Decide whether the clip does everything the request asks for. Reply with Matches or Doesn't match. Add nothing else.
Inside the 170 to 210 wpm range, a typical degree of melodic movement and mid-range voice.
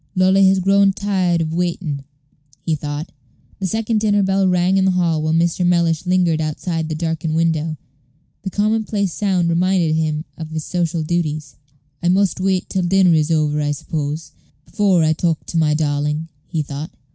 Matches